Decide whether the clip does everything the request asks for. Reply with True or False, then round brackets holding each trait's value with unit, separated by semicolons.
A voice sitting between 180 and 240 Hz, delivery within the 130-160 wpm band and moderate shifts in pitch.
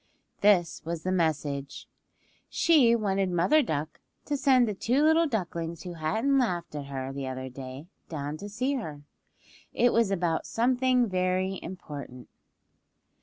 False (185 Hz; 145 wpm; 7.6 semitones)